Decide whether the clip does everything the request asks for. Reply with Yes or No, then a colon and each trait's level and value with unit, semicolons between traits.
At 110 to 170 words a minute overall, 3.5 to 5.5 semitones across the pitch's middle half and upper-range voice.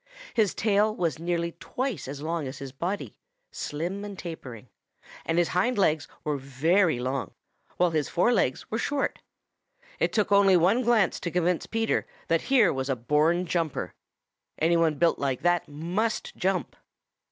No: average, 165 wpm; average, 5.2 semitones; medium, 170 Hz